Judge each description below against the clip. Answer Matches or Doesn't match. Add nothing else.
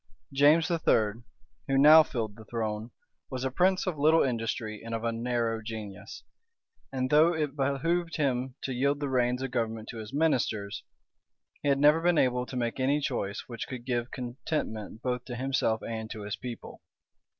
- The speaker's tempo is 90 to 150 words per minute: Doesn't match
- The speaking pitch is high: Doesn't match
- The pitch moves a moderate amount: Matches